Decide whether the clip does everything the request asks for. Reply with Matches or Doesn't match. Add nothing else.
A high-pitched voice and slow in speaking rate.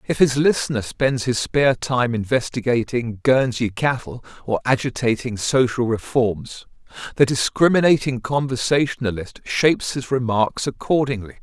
Doesn't match